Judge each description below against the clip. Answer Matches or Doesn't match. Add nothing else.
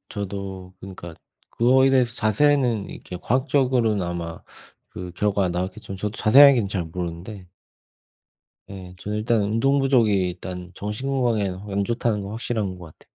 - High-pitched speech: Doesn't match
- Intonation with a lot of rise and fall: Doesn't match